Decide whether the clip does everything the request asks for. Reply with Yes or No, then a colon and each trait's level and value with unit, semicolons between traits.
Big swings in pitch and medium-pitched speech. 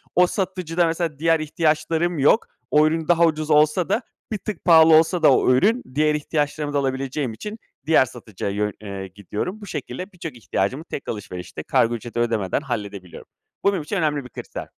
Yes: wide, 6.0 semitones; medium, 155 Hz